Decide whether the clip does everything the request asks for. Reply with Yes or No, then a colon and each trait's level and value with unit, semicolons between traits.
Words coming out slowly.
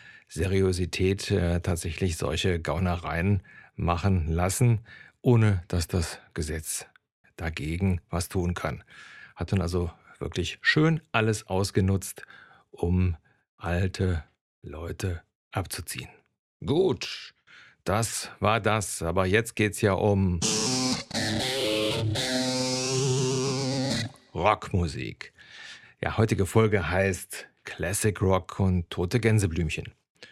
Yes: slow, 90 wpm